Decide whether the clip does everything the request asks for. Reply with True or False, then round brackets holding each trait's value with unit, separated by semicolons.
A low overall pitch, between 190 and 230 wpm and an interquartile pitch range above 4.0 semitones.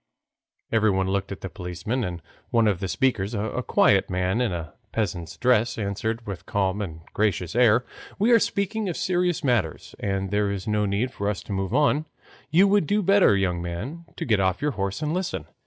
True (105 Hz; 205 wpm; 5.5 semitones)